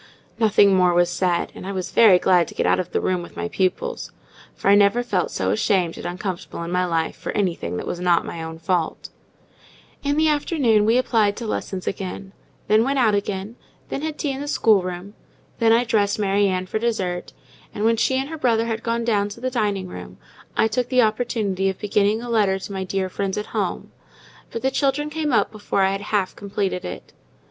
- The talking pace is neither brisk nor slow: No, fast, 220 wpm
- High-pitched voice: Yes, high, 205 Hz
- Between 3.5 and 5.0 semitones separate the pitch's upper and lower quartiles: Yes, average, 3.8 semitones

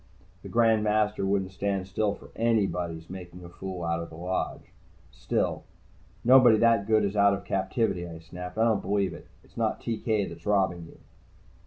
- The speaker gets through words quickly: No, average, 180 wpm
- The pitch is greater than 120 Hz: No, low, 100 Hz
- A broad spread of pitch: No, average, 3.3 semitones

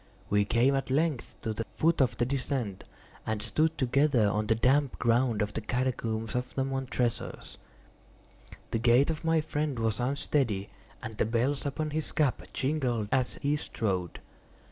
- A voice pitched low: Yes, low, 125 Hz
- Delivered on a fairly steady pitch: No, average, 3.9 semitones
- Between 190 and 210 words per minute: No, average, 165 wpm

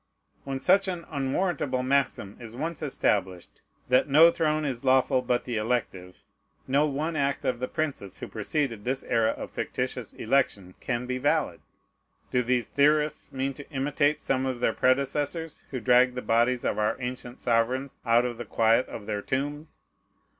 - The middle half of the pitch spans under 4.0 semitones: Yes, average, 3.3 semitones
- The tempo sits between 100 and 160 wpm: No, average, 170 wpm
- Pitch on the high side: No, low, 130 Hz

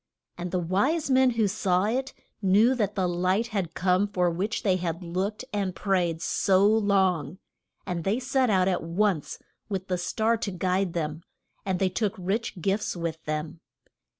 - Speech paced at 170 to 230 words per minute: Yes, average, 175 wpm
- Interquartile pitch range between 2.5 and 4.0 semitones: Yes, average, 3.0 semitones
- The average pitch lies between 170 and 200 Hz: Yes, high, 190 Hz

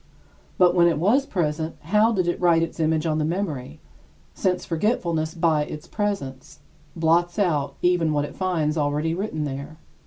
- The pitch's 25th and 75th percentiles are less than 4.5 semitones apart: Yes, average, 2.9 semitones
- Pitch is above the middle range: No, medium, 165 Hz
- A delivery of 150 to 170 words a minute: Yes, average, 165 wpm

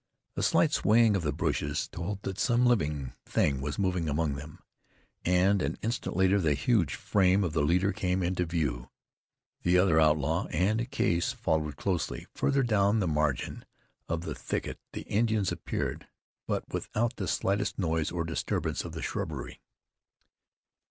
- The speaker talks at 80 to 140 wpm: No, average, 160 wpm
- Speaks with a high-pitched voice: No, very low, 90 Hz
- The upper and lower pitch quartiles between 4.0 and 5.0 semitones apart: Yes, average, 4.4 semitones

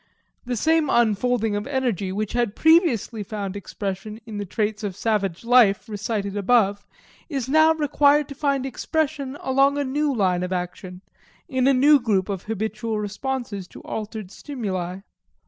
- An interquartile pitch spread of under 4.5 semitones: No, average, 5.0 semitones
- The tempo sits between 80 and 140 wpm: No, average, 155 wpm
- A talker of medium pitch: No, high, 220 Hz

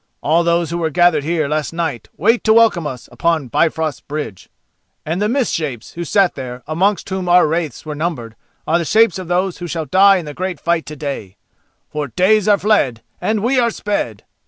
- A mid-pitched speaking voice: Yes, medium, 170 Hz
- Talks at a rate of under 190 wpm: No, fast, 205 wpm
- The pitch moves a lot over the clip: No, average, 4.1 semitones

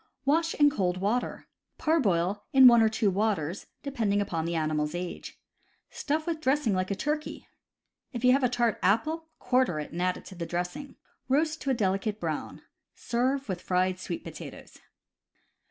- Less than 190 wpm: Yes, average, 170 wpm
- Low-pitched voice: No, high, 215 Hz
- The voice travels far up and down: Yes, wide, 6.9 semitones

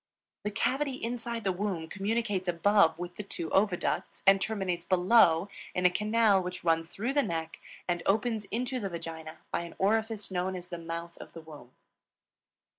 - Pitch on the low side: No, high, 190 Hz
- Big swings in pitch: No, average, 4.1 semitones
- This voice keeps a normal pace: Yes, average, 175 wpm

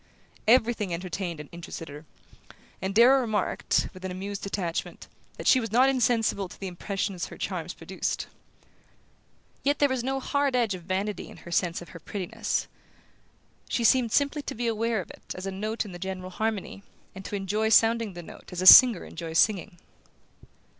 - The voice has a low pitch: No, high, 205 Hz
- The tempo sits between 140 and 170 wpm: No, average, 180 wpm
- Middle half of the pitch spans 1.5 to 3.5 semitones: No, average, 4.1 semitones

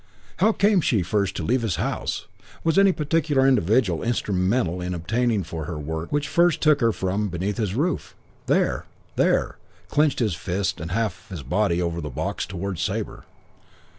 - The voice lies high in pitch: No, low, 100 Hz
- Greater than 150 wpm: Yes, average, 165 wpm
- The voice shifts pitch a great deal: Yes, wide, 7.2 semitones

